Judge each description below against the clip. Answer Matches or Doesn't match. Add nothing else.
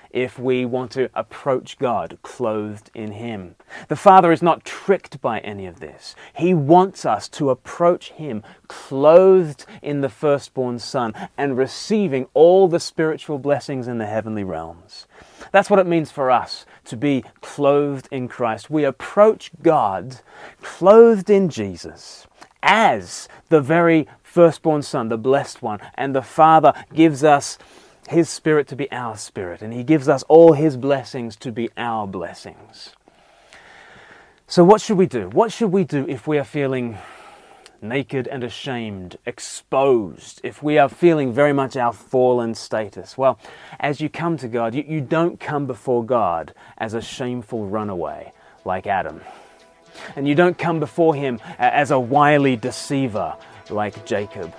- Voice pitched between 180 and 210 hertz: Doesn't match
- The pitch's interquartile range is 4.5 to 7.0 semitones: Matches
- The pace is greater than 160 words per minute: Doesn't match